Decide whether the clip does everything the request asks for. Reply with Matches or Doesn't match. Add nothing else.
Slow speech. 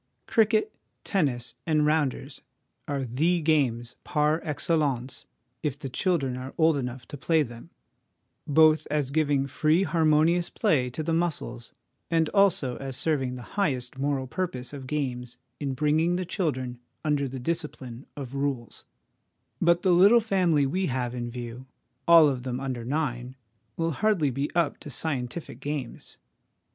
Doesn't match